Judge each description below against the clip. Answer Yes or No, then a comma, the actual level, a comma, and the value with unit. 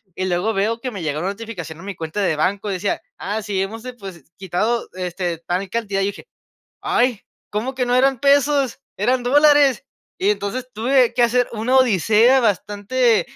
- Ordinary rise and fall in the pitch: Yes, average, 4.5 semitones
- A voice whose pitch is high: Yes, high, 220 Hz